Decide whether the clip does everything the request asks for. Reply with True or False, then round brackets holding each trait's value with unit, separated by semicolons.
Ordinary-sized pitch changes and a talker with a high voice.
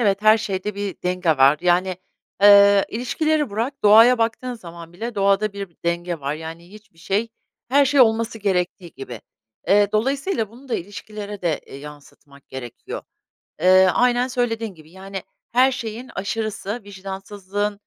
True (4.1 semitones; 200 Hz)